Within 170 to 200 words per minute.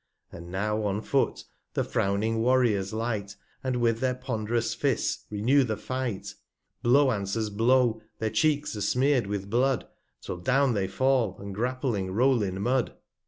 No: average, 160 wpm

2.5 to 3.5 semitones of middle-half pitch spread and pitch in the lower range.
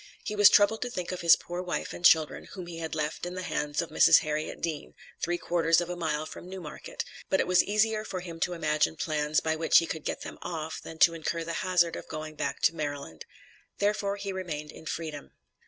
No: average, 2.9 semitones; medium, 170 Hz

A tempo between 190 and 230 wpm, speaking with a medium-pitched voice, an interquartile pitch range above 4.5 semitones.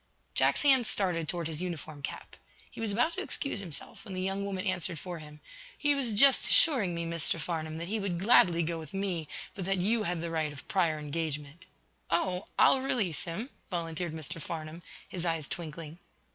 No: average, 195 wpm; medium, 175 Hz; average, 3.6 semitones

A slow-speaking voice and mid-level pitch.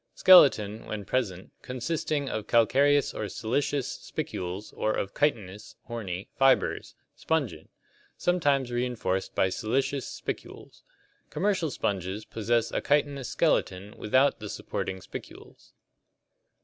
No: slow, 110 wpm; low, 120 Hz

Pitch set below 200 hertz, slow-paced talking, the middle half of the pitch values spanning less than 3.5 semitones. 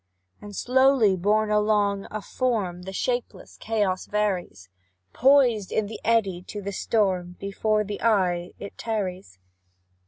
No: high, 205 Hz; slow, 130 wpm; narrow, 2.6 semitones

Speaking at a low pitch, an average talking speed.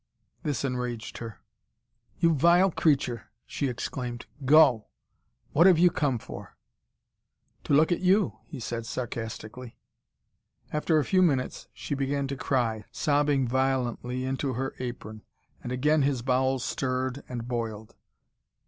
No: low, 130 Hz; slow, 130 wpm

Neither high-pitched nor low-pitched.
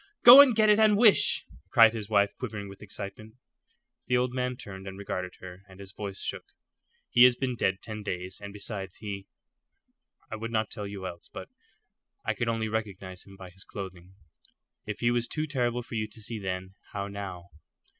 No: low, 105 Hz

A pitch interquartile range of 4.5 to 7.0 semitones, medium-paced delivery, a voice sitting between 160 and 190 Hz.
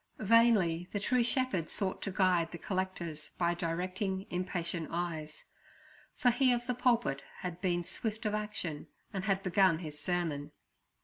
No: average, 3.9 semitones; average, 150 wpm; medium, 185 Hz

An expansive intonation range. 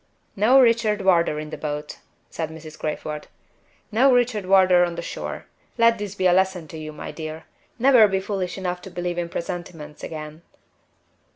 No: average, 4.5 semitones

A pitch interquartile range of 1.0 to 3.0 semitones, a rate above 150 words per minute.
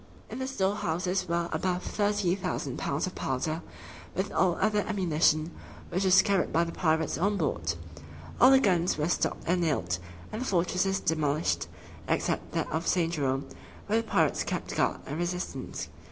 No: average, 3.4 semitones; average, 170 wpm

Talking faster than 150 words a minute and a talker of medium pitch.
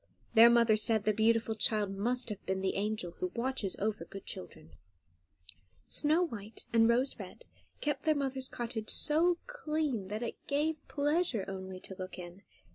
No: average, 165 wpm; high, 230 Hz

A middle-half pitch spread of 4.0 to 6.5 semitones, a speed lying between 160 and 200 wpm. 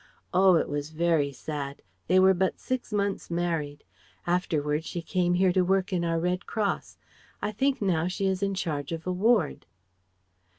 No: average, 3.0 semitones; average, 175 wpm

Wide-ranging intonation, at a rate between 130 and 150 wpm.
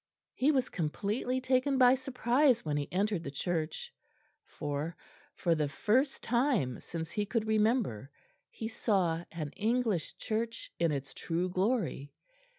Yes: wide, 7.3 semitones; average, 140 wpm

